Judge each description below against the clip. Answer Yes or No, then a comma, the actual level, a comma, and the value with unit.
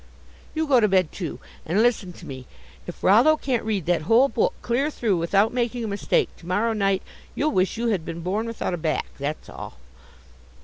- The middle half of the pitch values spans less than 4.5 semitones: No, average, 5.0 semitones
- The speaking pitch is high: Yes, high, 205 Hz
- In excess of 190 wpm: Yes, fast, 205 wpm